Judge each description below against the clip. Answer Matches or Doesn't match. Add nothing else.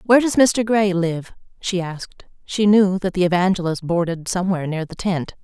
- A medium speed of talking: Matches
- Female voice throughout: Matches